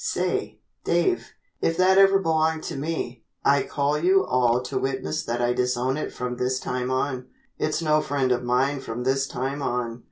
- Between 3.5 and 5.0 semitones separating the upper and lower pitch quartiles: Yes, average, 3.8 semitones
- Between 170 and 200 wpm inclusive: Yes, average, 185 wpm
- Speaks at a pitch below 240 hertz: Yes, low, 135 Hz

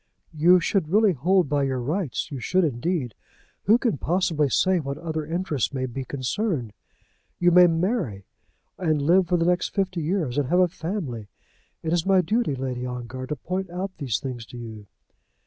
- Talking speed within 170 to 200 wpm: Yes, average, 180 wpm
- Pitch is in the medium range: Yes, medium, 160 Hz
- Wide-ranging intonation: Yes, wide, 5.8 semitones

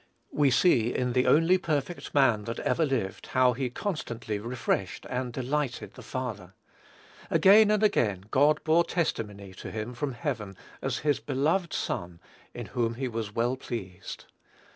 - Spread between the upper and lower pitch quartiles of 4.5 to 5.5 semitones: Yes, average, 4.9 semitones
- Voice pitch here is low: Yes, low, 125 Hz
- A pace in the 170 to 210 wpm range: No, average, 155 wpm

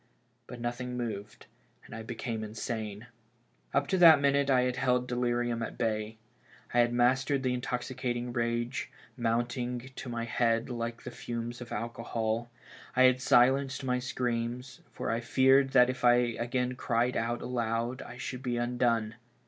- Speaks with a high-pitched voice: No, low, 120 Hz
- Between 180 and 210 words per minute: No, average, 155 wpm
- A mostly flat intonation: Yes, narrow, 1.4 semitones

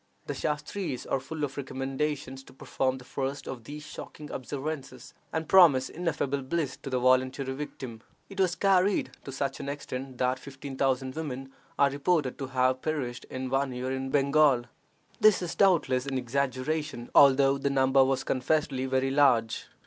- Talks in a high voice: No, low, 135 Hz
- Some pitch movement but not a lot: No, narrow, 2.3 semitones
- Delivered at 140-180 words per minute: Yes, average, 165 wpm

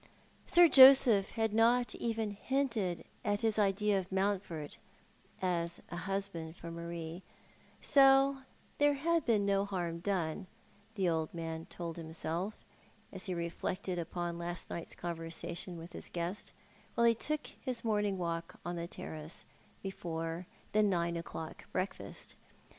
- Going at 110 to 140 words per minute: Yes, slow, 135 wpm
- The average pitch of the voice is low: No, medium, 185 Hz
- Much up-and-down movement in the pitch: No, average, 4.2 semitones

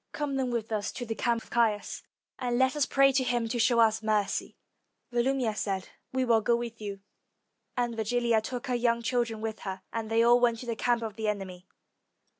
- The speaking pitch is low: No, high, 235 Hz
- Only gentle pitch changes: Yes, narrow, 2.0 semitones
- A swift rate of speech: Yes, fast, 215 wpm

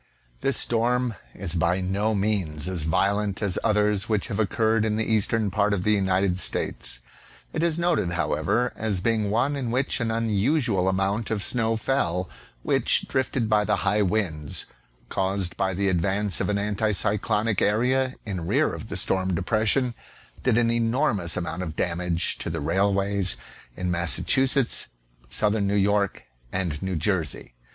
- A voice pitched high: No, low, 100 Hz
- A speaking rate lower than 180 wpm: Yes, average, 160 wpm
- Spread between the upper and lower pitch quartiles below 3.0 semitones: No, average, 3.5 semitones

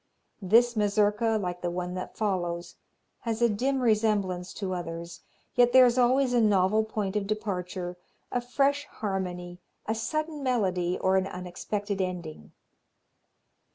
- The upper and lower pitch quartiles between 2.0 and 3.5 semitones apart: No, average, 4.5 semitones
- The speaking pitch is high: Yes, high, 205 Hz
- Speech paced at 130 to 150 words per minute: Yes, average, 140 wpm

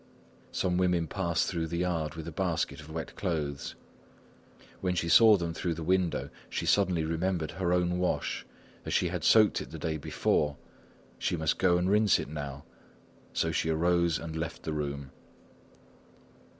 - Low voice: Yes, very low, 85 Hz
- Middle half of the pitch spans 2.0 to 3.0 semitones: Yes, narrow, 2.4 semitones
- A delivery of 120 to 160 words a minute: No, average, 170 wpm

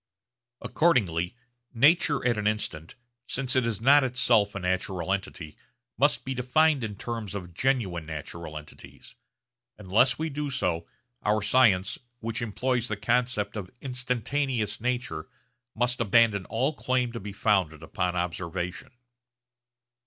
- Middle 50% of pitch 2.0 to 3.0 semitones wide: No, average, 5.3 semitones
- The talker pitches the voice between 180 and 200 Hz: No, low, 110 Hz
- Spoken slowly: Yes, slow, 130 wpm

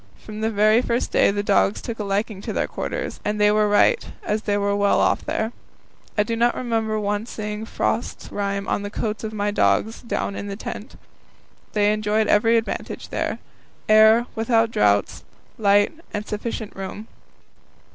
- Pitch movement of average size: No, narrow, 1.5 semitones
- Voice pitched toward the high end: Yes, high, 210 Hz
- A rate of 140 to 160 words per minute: No, average, 175 wpm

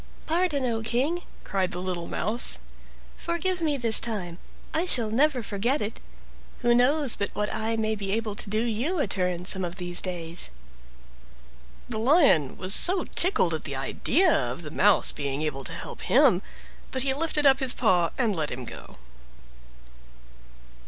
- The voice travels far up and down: Yes, wide, 7.3 semitones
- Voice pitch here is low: No, high, 220 Hz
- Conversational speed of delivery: Yes, average, 170 wpm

